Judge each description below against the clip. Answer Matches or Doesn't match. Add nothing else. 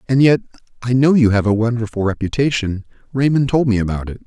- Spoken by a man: Matches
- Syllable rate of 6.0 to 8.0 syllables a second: Matches